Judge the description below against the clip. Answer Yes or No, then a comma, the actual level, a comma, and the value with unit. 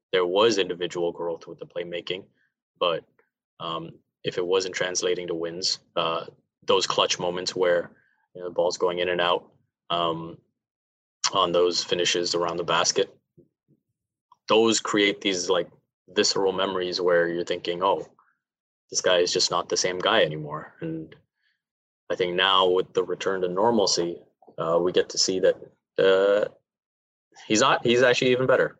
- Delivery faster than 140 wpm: Yes, average, 160 wpm